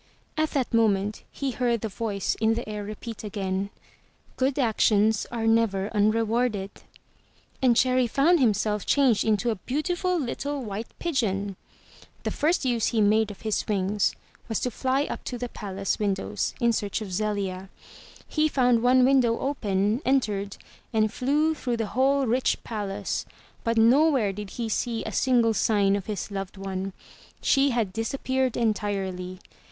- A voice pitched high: Yes, high, 225 Hz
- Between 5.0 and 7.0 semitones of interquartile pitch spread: No, average, 3.9 semitones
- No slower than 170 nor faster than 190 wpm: No, average, 155 wpm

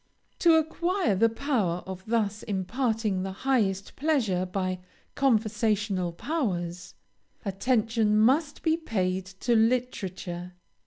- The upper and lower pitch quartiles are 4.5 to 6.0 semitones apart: Yes, average, 5.2 semitones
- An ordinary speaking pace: No, slow, 105 wpm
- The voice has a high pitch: Yes, high, 215 Hz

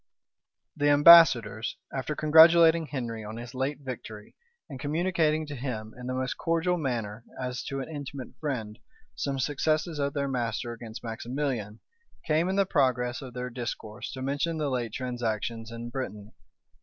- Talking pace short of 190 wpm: Yes, average, 155 wpm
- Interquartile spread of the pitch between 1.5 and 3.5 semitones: No, average, 4.2 semitones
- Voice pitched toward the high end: No, low, 130 Hz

